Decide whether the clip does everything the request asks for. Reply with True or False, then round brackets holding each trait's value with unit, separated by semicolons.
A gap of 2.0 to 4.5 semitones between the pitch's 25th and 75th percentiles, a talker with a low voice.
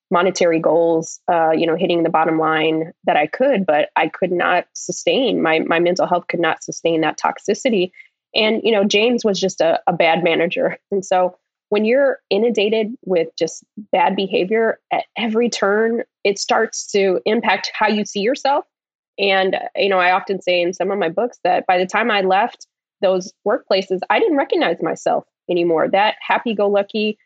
False (3.8 semitones; 190 Hz)